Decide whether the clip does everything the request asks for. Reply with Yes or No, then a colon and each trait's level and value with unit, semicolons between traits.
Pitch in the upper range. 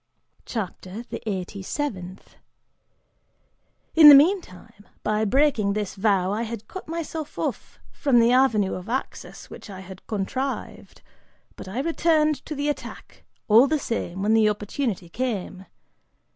Yes: high, 225 Hz